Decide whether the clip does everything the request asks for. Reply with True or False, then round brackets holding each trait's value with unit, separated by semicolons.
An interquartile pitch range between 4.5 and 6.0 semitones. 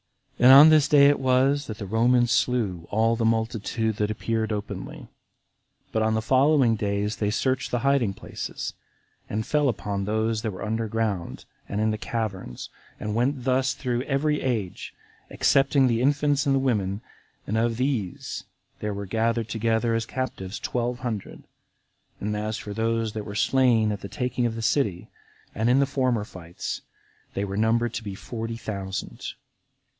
False (3.3 semitones)